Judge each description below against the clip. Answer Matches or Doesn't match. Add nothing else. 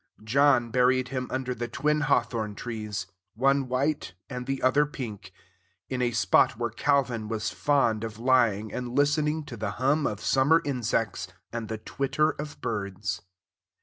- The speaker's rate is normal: Matches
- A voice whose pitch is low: Matches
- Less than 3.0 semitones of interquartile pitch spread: Doesn't match